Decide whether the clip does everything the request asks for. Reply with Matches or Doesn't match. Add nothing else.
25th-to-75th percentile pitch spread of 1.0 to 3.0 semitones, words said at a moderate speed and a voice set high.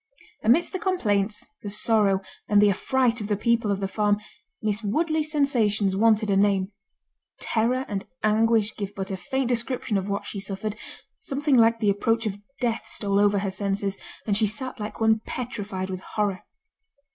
Matches